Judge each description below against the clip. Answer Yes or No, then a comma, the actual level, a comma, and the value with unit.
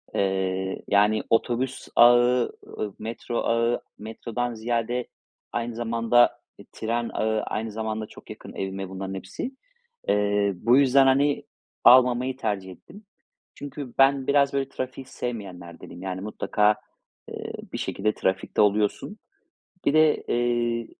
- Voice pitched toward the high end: No, low, 115 Hz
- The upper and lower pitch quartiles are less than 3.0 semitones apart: No, average, 3.4 semitones